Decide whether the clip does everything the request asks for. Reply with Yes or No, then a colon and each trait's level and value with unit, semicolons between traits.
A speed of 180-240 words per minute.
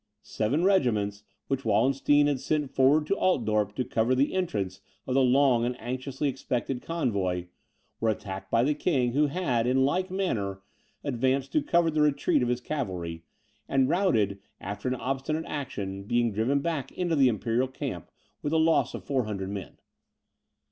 No: average, 165 wpm